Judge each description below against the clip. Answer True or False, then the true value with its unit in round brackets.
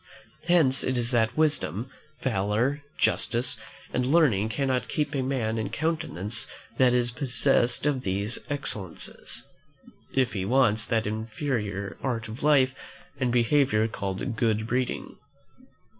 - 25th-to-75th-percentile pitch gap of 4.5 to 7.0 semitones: False (3.6 semitones)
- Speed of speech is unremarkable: False (130 wpm)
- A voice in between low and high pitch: False (120 Hz)